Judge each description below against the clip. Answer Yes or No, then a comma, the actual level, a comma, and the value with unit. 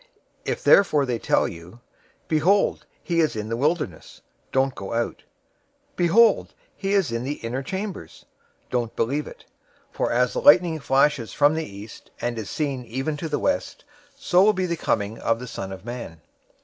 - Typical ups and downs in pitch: No, wide, 6.6 semitones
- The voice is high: No, low, 135 Hz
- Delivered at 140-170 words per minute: No, average, 185 wpm